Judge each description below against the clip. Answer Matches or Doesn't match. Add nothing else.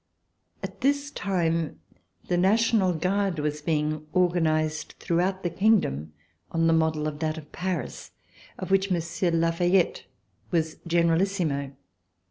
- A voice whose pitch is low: Doesn't match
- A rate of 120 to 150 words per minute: Matches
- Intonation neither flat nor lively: Matches